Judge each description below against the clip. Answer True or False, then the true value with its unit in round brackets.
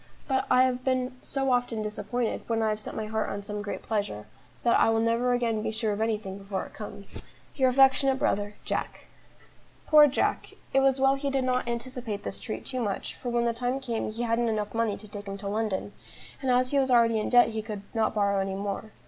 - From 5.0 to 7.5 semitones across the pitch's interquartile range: False (3.2 semitones)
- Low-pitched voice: False (230 Hz)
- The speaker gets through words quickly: True (230 wpm)